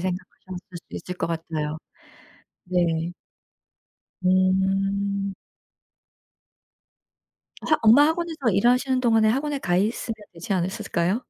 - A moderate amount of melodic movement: Yes, average, 4.9 semitones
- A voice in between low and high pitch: No, high, 195 Hz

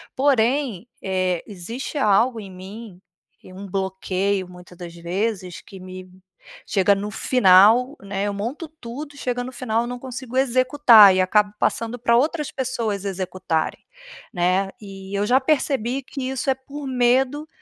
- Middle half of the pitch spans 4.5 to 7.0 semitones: Yes, average, 5.2 semitones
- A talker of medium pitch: No, high, 220 Hz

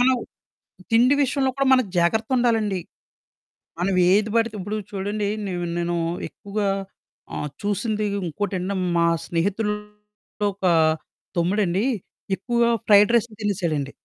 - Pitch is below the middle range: No, high, 205 Hz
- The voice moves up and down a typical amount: Yes, average, 3.1 semitones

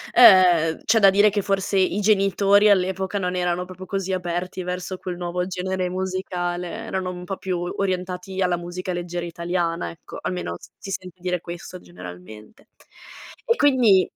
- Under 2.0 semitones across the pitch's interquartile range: Yes, narrow, 1.5 semitones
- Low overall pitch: No, medium, 185 Hz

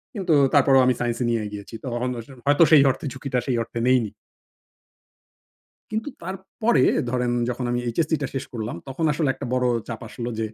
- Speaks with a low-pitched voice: Yes, low, 130 Hz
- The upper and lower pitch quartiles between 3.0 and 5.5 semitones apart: Yes, average, 3.6 semitones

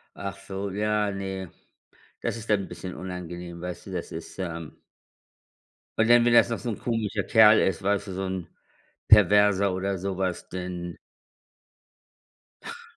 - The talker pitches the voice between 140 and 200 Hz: No, very low, 95 Hz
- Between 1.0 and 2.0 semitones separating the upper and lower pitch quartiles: No, narrow, 2.4 semitones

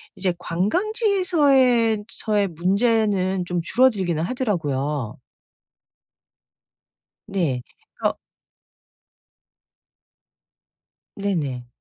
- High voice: Yes, high, 195 Hz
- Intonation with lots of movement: Yes, wide, 6.3 semitones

